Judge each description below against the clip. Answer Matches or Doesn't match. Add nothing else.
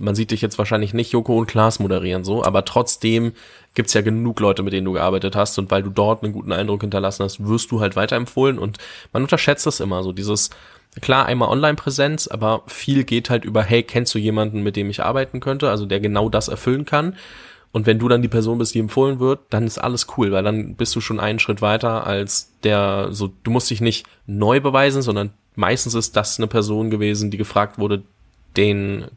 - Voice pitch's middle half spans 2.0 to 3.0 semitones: Matches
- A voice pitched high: Doesn't match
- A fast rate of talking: Matches